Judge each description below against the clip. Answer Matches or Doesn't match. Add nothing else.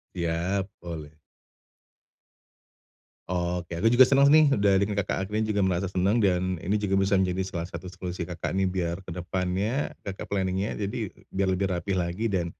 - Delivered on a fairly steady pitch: Matches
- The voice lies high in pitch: Doesn't match